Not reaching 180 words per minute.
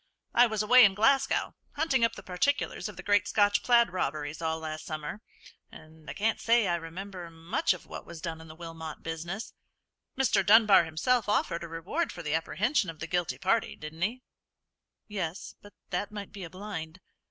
No: average, 190 wpm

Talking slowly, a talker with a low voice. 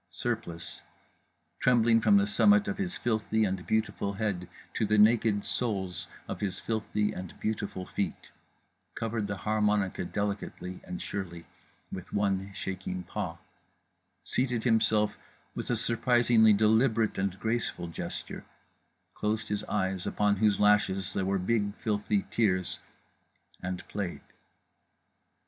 Yes: slow, 125 wpm; low, 105 Hz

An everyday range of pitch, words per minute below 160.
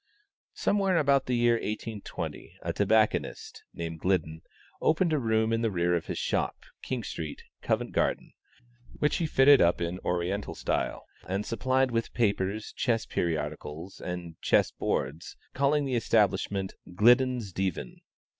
No: wide, 6.2 semitones; average, 140 wpm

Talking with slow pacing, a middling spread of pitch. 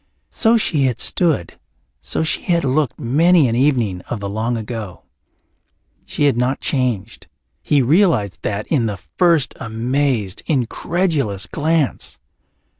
No: slow, 130 wpm; wide, 5.9 semitones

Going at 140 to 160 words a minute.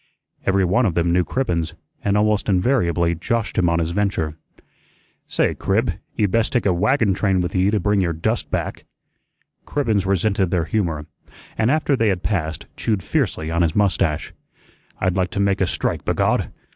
No: average, 175 wpm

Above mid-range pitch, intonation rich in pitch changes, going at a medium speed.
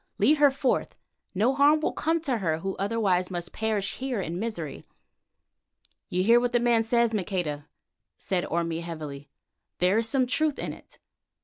Yes: high, 215 Hz; wide, 5.9 semitones; average, 170 wpm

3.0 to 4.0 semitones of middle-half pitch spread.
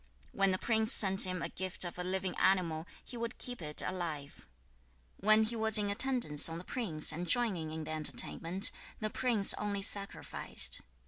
No: average, 4.7 semitones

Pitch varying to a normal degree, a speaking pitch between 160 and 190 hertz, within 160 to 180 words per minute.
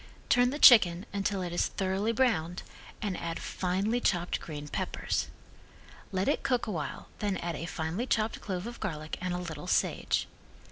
Yes: average, 4.1 semitones; medium, 185 Hz; average, 170 wpm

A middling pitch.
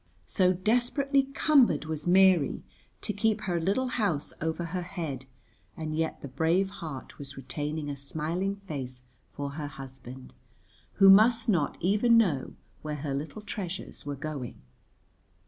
Yes: medium, 165 Hz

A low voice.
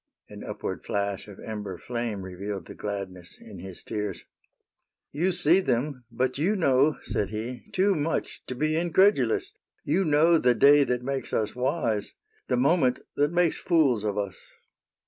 Yes: low, 125 Hz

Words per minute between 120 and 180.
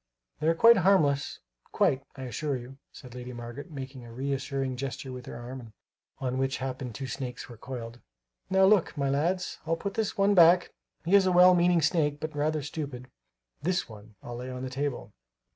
No: average, 195 wpm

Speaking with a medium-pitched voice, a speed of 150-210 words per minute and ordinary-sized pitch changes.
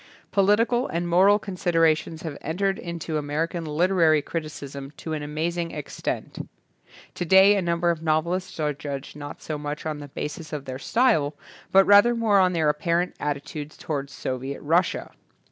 Yes: medium, 165 Hz; average, 160 wpm; average, 3.5 semitones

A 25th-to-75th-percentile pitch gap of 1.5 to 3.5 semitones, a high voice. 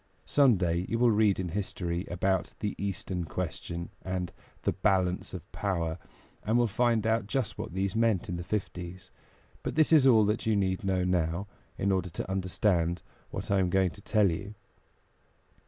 No: average, 3.1 semitones; very low, 95 Hz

